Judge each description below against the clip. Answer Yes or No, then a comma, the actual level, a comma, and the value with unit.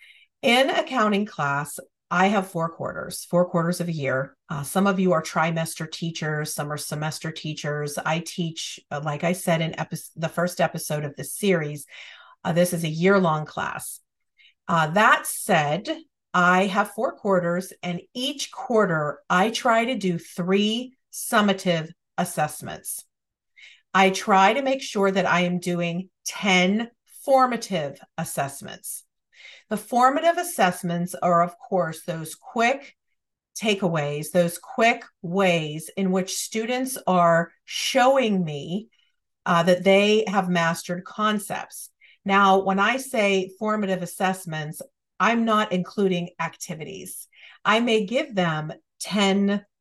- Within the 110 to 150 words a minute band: Yes, slow, 135 wpm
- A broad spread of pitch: No, average, 4.2 semitones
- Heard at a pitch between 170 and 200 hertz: Yes, medium, 185 Hz